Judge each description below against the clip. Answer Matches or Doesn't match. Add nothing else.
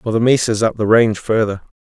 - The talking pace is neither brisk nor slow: Doesn't match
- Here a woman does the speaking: Doesn't match